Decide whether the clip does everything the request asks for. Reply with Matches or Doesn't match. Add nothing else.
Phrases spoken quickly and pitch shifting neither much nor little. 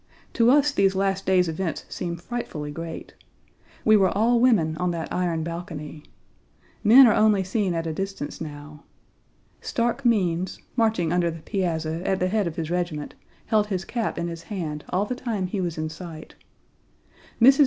Doesn't match